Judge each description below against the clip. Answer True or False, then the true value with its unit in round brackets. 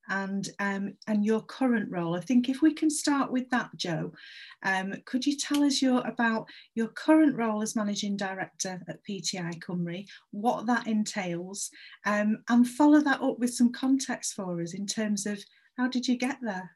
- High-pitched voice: True (220 Hz)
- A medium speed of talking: True (185 wpm)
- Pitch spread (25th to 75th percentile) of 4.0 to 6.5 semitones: True (4.3 semitones)